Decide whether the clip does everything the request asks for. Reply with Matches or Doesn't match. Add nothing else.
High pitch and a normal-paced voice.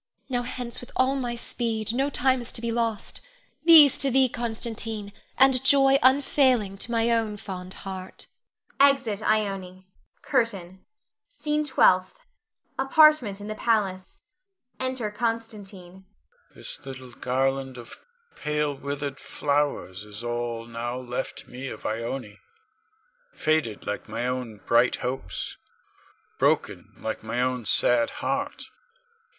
Doesn't match